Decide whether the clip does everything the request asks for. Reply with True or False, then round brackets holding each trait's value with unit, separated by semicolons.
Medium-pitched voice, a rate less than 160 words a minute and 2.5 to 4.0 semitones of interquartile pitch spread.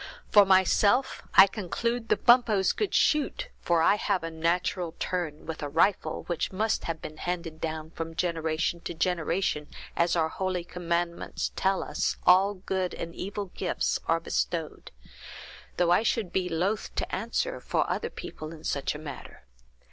False (175 Hz; 165 wpm; 3.0 semitones)